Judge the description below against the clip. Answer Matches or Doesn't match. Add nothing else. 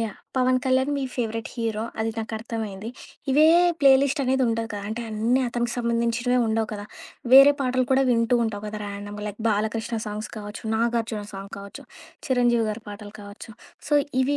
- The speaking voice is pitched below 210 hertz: Doesn't match